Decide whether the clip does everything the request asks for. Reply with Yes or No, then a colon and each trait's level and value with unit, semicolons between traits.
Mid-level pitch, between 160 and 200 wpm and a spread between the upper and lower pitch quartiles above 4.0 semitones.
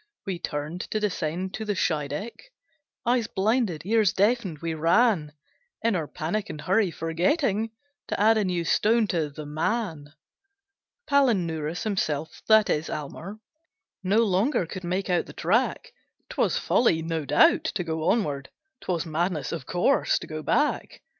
No: medium, 180 Hz; average, 150 wpm; average, 5.3 semitones